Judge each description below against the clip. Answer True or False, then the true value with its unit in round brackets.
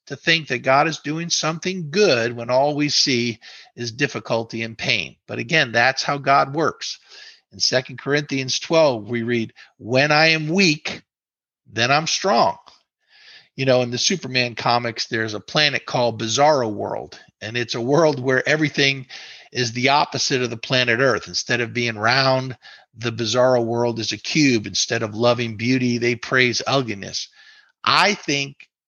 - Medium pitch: False (130 Hz)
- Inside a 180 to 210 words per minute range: False (165 wpm)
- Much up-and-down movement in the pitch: False (3.8 semitones)